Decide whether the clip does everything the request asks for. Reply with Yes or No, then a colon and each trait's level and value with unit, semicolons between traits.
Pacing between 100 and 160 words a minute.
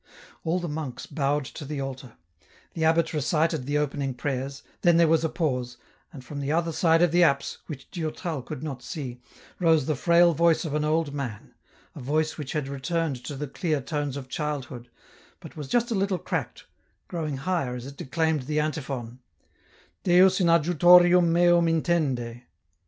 No: average, 180 wpm